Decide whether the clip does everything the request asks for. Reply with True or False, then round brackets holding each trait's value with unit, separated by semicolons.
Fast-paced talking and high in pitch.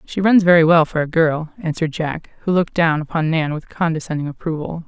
False (210 wpm; 160 Hz)